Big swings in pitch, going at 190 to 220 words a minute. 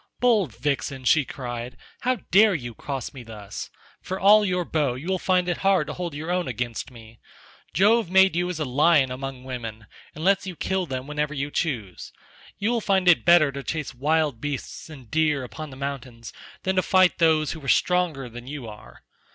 Yes: wide, 5.8 semitones; average, 200 wpm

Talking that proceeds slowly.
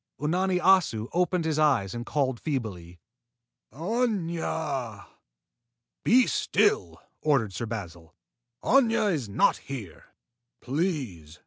Yes: slow, 100 wpm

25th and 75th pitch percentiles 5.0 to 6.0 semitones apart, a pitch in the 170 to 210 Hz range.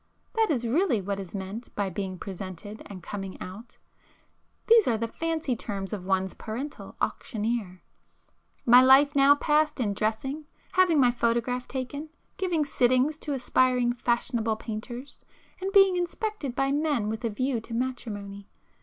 No: wide, 5.4 semitones; high, 245 Hz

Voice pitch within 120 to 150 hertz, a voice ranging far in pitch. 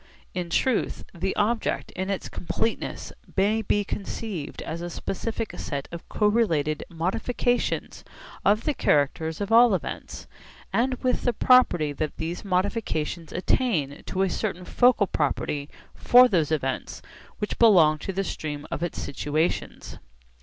No: medium, 185 Hz; wide, 5.8 semitones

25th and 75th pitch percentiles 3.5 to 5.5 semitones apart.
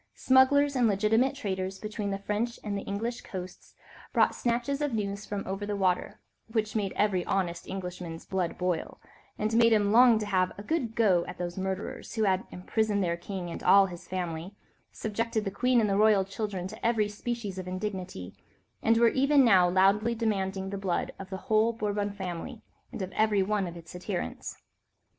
No: average, 3.0 semitones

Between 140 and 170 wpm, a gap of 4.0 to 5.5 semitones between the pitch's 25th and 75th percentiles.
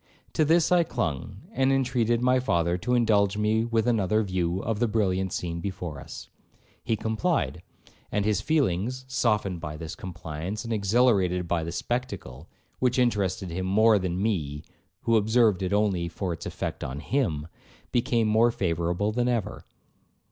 Yes: average, 160 wpm; average, 5.1 semitones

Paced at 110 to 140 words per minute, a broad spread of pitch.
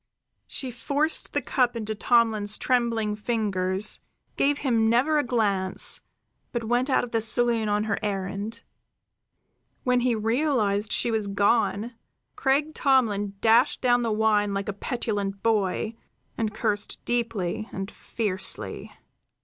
No: slow, 135 wpm; average, 2.9 semitones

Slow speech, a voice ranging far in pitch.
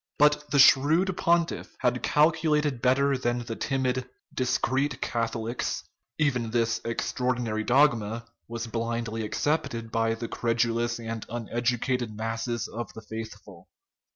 No: slow, 125 wpm; average, 3.0 semitones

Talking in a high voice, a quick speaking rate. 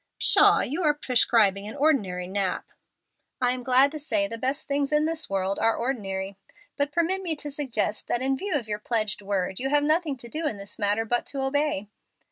Yes: very high, 250 Hz; fast, 210 wpm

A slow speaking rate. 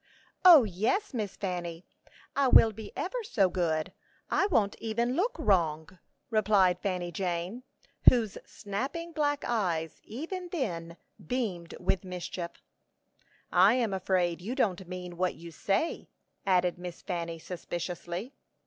Yes: slow, 130 wpm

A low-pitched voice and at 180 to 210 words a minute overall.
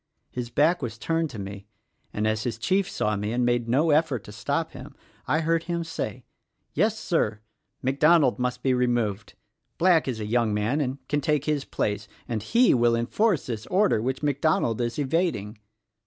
Yes: low, 125 Hz; average, 185 wpm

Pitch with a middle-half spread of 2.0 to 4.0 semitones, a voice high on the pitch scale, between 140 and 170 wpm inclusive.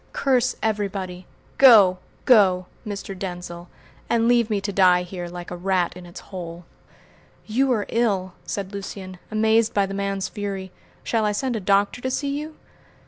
Yes: average, 3.4 semitones; high, 200 Hz; average, 165 wpm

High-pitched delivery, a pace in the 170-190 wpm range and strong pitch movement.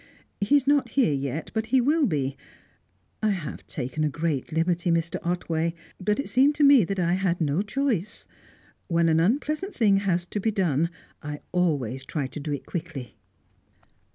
No: medium, 175 Hz; average, 180 wpm; wide, 6.2 semitones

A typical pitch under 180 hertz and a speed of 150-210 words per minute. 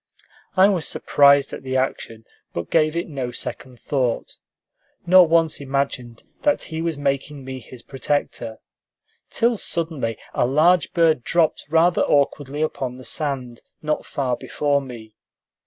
No: medium, 140 Hz; average, 140 wpm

